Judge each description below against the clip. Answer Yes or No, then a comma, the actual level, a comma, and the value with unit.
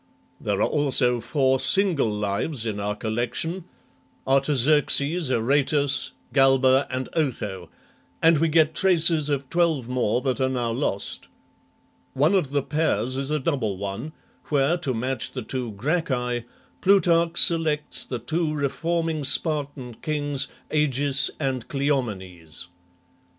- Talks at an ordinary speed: No, slow, 125 wpm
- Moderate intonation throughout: Yes, average, 3.9 semitones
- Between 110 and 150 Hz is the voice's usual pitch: Yes, low, 135 Hz